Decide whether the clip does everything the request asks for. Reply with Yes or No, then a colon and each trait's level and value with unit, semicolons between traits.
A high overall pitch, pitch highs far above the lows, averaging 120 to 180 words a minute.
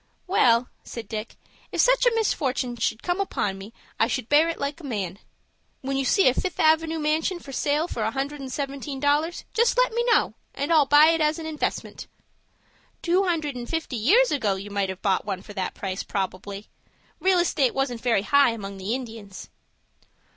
No: very high, 275 Hz; wide, 6.7 semitones; average, 195 wpm